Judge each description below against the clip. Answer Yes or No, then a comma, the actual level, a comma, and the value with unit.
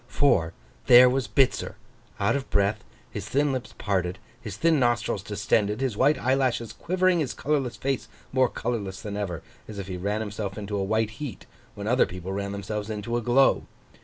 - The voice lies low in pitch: Yes, low, 110 Hz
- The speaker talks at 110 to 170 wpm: No, average, 185 wpm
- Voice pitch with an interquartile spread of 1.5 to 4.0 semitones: No, average, 4.5 semitones